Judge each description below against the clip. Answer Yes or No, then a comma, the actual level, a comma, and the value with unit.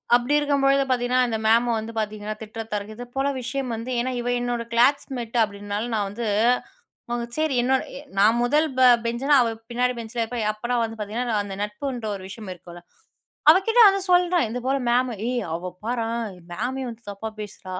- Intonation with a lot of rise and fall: No, average, 2.9 semitones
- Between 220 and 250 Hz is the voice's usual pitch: Yes, high, 240 Hz